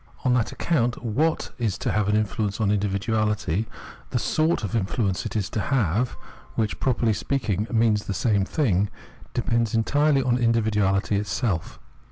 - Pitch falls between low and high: No, low, 110 Hz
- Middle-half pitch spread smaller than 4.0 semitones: Yes, average, 2.8 semitones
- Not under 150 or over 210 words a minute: Yes, average, 165 wpm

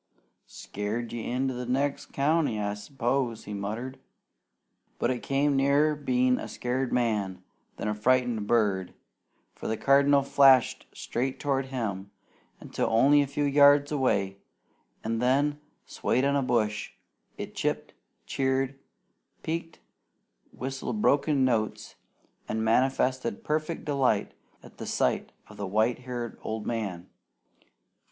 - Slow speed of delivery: Yes, slow, 130 wpm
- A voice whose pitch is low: Yes, low, 130 Hz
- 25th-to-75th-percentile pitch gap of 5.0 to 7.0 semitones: No, average, 3.9 semitones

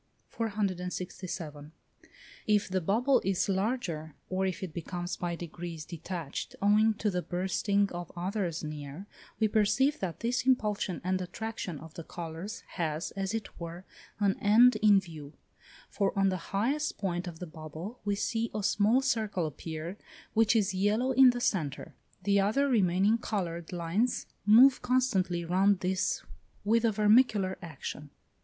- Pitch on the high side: Yes, high, 195 Hz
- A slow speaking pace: No, average, 150 wpm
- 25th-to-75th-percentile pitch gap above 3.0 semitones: Yes, average, 3.9 semitones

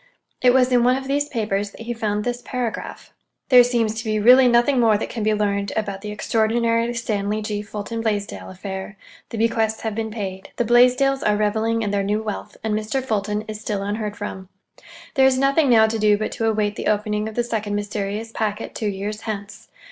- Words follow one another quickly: Yes, fast, 210 wpm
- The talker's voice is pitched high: Yes, high, 220 Hz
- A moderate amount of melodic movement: No, narrow, 2.2 semitones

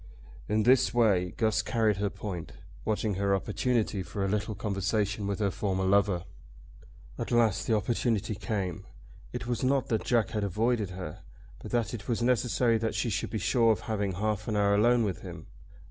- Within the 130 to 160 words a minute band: No, average, 185 wpm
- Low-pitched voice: Yes, low, 105 Hz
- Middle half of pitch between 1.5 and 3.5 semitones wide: Yes, narrow, 2.6 semitones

